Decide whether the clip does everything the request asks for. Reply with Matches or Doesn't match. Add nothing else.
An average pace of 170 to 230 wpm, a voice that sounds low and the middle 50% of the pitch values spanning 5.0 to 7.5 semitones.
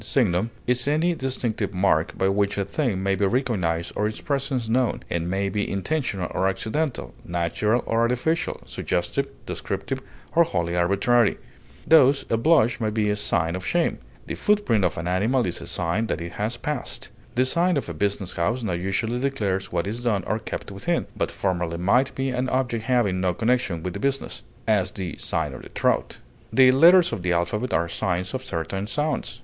Matches